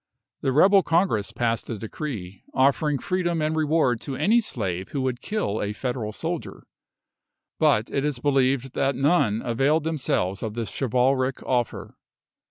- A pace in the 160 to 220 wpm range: No, average, 150 wpm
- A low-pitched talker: Yes, low, 130 Hz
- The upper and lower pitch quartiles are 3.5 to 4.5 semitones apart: No, average, 5.1 semitones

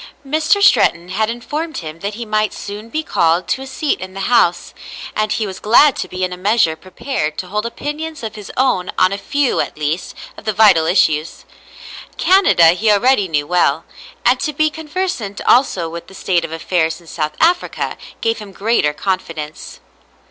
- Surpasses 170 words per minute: Yes, average, 190 wpm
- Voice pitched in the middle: No, high, 205 Hz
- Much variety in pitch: Yes, wide, 6.9 semitones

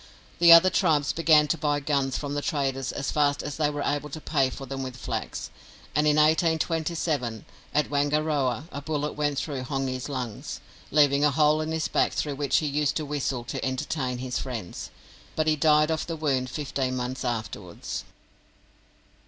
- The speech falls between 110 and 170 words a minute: No, average, 180 wpm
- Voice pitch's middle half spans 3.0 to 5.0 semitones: No, narrow, 2.5 semitones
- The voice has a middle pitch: Yes, medium, 145 Hz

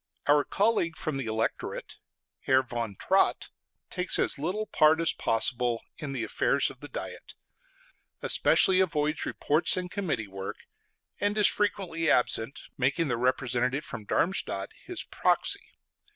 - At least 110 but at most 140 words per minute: Yes, slow, 135 wpm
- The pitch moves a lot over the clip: Yes, wide, 6.7 semitones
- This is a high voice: No, medium, 150 Hz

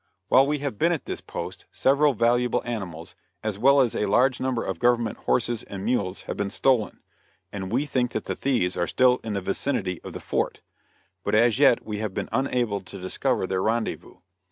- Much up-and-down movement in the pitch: No, average, 4.5 semitones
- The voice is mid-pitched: No, low, 115 Hz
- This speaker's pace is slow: No, average, 200 wpm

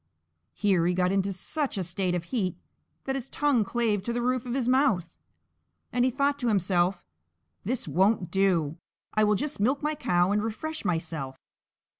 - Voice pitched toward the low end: No, high, 205 Hz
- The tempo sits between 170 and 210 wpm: Yes, average, 180 wpm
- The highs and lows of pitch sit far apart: Yes, wide, 6.0 semitones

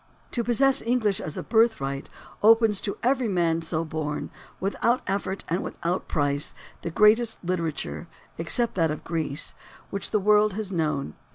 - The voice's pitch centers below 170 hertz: No, high, 190 Hz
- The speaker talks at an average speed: Yes, average, 155 wpm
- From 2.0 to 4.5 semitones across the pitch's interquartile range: No, wide, 5.6 semitones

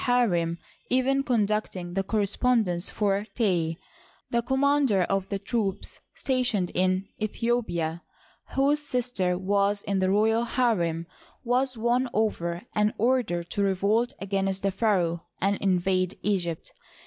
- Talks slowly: Yes, slow, 125 wpm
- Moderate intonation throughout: Yes, average, 4.5 semitones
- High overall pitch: Yes, high, 200 Hz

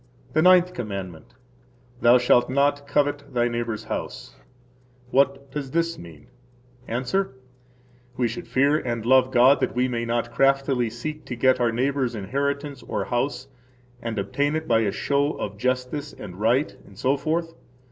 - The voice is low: Yes, low, 130 Hz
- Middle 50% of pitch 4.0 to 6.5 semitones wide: No, average, 3.3 semitones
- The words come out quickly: No, average, 150 wpm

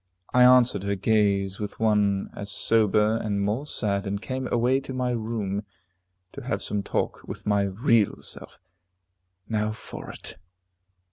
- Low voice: Yes, low, 105 Hz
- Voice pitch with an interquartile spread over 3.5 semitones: No, average, 2.9 semitones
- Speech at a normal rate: Yes, average, 150 wpm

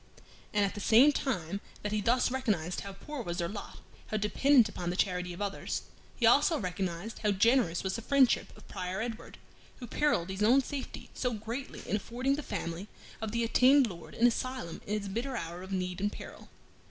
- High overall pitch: Yes, high, 210 Hz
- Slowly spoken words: No, average, 200 wpm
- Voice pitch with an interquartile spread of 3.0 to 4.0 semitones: No, average, 4.9 semitones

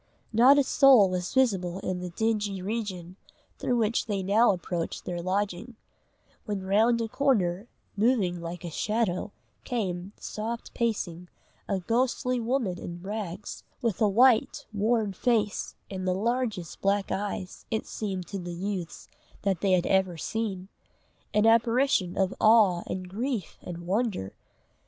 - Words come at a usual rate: Yes, average, 145 wpm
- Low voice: No, high, 200 Hz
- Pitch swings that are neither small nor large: Yes, average, 3.9 semitones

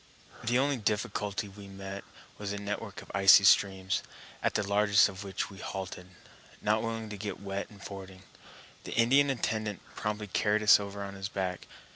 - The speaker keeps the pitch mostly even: Yes, narrow, 1.6 semitones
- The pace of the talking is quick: No, average, 175 wpm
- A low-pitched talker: Yes, low, 100 Hz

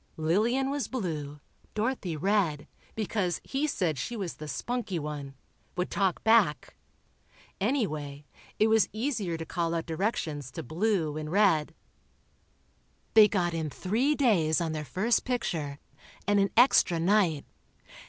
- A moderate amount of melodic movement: No, wide, 5.9 semitones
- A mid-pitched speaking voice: Yes, medium, 180 Hz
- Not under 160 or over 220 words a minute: No, slow, 135 wpm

